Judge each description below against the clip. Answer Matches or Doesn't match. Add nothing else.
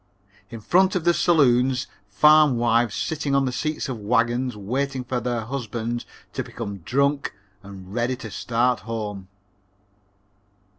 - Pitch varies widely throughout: Doesn't match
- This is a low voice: Matches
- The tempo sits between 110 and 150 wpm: Matches